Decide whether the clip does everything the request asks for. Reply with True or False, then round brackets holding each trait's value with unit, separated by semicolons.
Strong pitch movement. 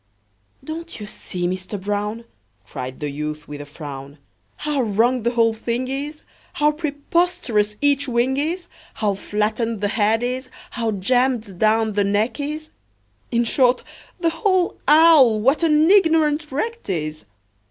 True (6.4 semitones)